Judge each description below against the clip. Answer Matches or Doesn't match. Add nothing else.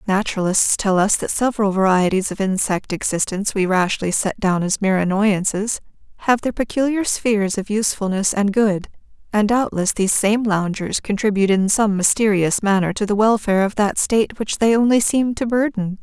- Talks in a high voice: Matches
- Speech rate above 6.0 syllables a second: Doesn't match